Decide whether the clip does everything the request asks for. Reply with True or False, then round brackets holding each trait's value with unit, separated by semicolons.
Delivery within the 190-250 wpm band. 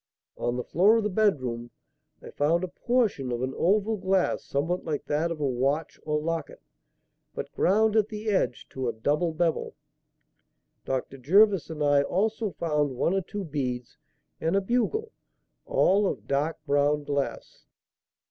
False (160 wpm)